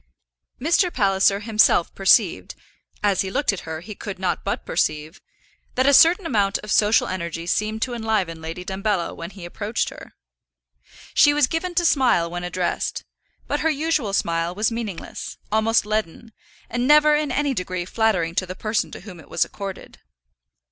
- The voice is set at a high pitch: Yes, high, 210 Hz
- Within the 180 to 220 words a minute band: No, average, 170 wpm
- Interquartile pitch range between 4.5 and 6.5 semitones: Yes, average, 5.2 semitones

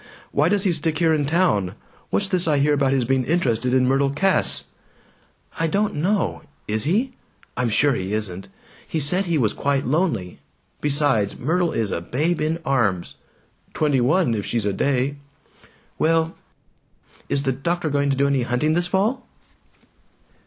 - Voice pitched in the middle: Yes, medium, 145 Hz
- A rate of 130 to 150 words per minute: No, average, 165 wpm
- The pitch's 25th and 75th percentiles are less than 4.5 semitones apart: No, average, 5.1 semitones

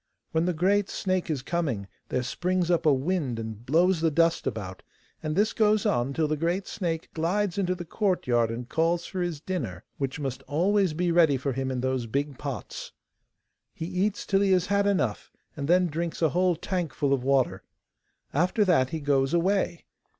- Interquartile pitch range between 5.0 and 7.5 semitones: Yes, average, 5.3 semitones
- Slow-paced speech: No, average, 190 wpm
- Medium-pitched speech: Yes, medium, 165 Hz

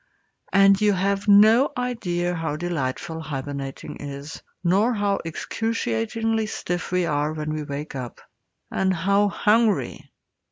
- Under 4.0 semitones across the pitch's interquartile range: No, average, 5.3 semitones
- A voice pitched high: No, medium, 175 Hz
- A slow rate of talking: Yes, slow, 125 wpm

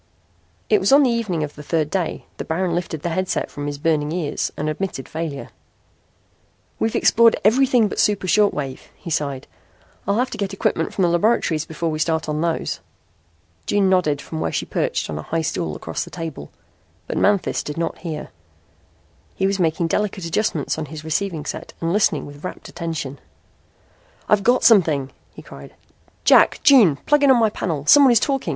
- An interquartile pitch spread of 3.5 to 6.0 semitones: Yes, average, 5.1 semitones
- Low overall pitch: No, medium, 170 Hz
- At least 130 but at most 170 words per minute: No, average, 190 wpm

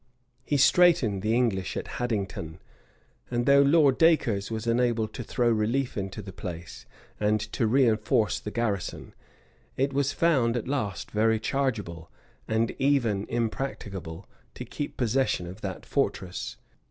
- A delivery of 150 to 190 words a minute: No, average, 140 wpm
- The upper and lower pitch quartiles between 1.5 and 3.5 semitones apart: No, average, 4.5 semitones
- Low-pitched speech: Yes, low, 115 Hz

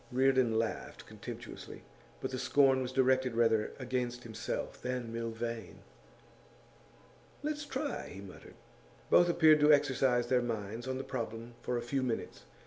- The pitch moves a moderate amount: No, narrow, 2.3 semitones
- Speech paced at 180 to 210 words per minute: No, average, 140 wpm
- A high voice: No, low, 125 Hz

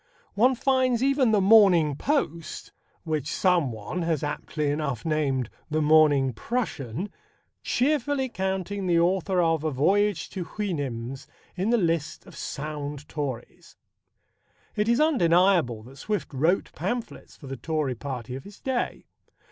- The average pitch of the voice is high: No, medium, 165 Hz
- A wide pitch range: Yes, wide, 6.2 semitones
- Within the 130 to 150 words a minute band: Yes, slow, 135 wpm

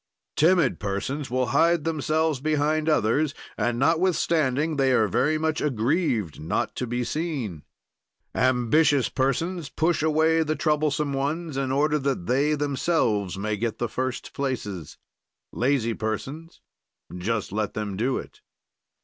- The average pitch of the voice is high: No, medium, 140 Hz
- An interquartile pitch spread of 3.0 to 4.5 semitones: No, average, 4.9 semitones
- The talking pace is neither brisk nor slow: No, slow, 130 wpm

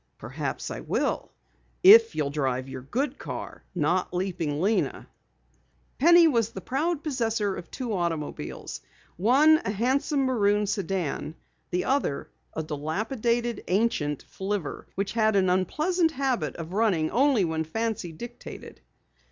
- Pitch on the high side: Yes, high, 205 Hz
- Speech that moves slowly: Yes, slow, 130 wpm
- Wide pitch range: Yes, wide, 6.8 semitones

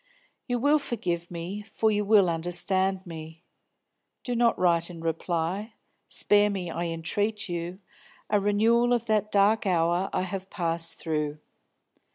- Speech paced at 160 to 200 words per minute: No, average, 145 wpm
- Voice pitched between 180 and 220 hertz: Yes, high, 190 Hz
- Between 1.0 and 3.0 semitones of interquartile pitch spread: No, average, 3.7 semitones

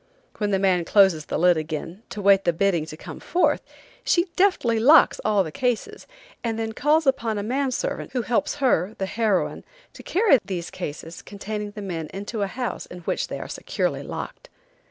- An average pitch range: No, wide, 5.7 semitones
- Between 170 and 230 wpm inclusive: Yes, average, 190 wpm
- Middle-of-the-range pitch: No, high, 210 Hz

